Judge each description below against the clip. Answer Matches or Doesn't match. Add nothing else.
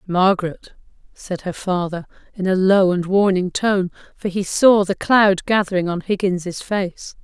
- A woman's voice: Matches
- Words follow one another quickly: Doesn't match